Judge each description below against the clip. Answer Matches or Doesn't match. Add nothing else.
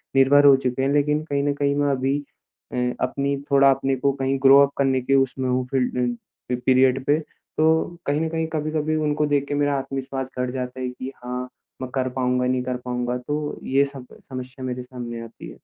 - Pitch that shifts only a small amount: Matches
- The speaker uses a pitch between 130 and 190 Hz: Matches